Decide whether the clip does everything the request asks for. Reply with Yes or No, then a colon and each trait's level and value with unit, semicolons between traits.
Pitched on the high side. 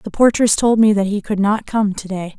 Yes: high, 205 Hz